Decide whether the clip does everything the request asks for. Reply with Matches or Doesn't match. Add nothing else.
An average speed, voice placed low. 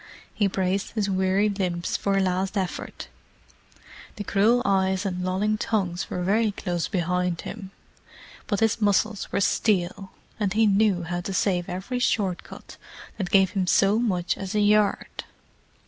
Doesn't match